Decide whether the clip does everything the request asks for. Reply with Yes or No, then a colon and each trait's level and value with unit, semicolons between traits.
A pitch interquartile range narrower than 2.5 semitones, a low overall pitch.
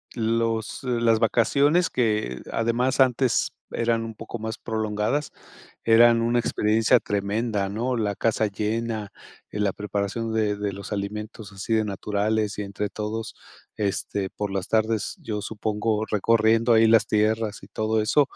Yes: narrow, 1.8 semitones; low, 110 Hz